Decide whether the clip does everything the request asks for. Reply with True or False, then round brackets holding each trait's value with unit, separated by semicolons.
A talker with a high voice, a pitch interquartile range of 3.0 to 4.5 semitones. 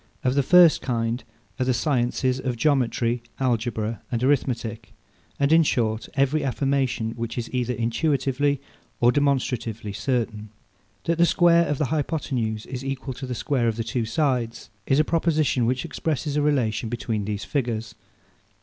False (125 Hz; 3.6 semitones)